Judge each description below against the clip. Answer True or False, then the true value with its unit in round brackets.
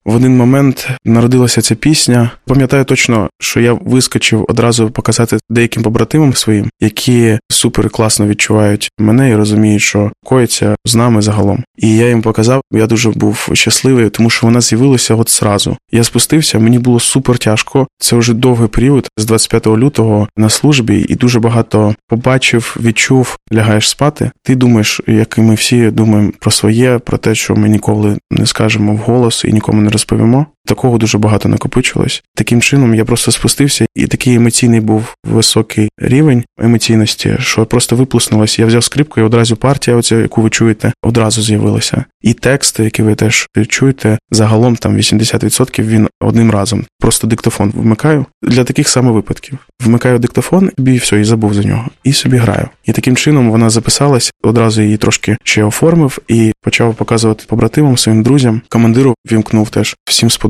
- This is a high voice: False (115 Hz)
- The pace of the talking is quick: True (165 wpm)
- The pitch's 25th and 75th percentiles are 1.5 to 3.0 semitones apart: True (2.4 semitones)